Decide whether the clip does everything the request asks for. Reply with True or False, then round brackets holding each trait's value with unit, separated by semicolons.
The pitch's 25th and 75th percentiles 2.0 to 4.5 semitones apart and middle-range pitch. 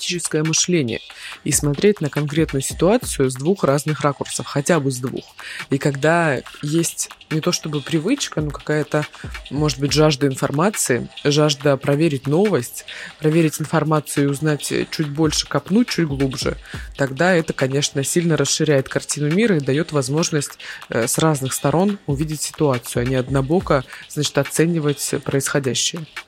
True (2.4 semitones; 150 Hz)